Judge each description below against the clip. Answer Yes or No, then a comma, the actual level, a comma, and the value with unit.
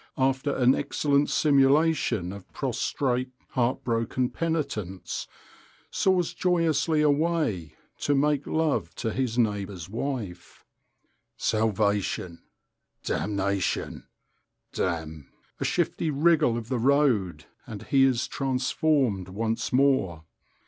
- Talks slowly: Yes, slow, 100 wpm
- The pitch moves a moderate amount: No, wide, 6.0 semitones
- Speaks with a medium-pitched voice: No, low, 125 Hz